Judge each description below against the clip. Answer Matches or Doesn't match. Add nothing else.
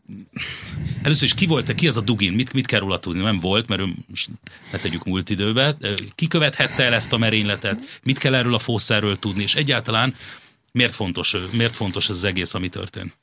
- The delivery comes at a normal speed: Doesn't match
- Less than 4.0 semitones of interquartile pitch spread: Doesn't match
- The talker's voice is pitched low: Matches